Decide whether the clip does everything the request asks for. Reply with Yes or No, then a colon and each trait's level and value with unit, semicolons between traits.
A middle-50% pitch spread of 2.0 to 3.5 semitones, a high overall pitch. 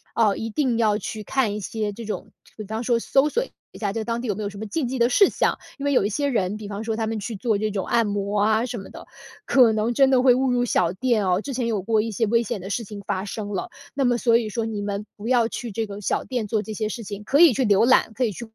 Yes: average, 2.8 semitones; high, 220 Hz